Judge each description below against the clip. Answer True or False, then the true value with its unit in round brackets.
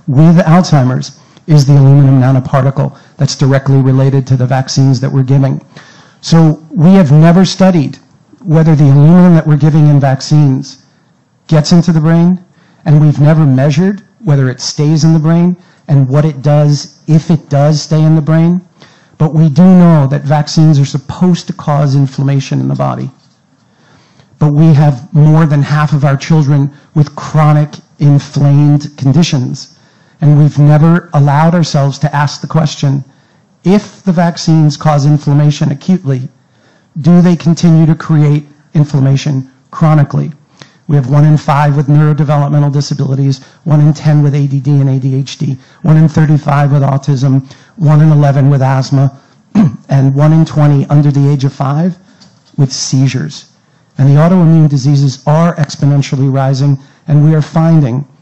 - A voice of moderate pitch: True (150 Hz)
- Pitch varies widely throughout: False (2.5 semitones)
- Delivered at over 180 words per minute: False (155 wpm)